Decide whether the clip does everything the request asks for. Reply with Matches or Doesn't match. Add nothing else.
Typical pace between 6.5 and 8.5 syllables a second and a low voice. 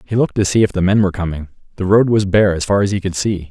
Matches